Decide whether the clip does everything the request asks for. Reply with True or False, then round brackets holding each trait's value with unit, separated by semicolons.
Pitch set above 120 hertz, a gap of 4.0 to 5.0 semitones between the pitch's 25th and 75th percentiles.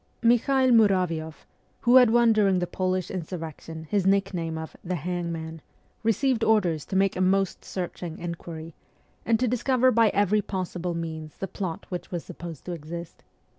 True (185 Hz; 4.3 semitones)